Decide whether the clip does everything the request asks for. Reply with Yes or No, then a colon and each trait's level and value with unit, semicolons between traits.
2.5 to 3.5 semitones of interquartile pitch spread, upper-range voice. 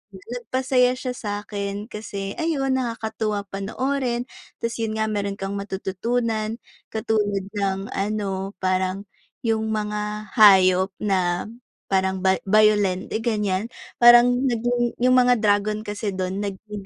Yes: average, 2.9 semitones; high, 210 Hz